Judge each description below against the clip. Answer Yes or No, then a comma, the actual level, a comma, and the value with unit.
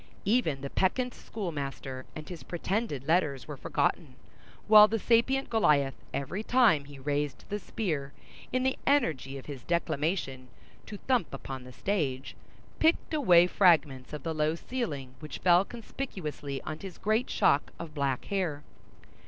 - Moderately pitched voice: Yes, medium, 165 Hz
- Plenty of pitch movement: Yes, wide, 7.2 semitones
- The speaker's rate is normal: Yes, average, 150 wpm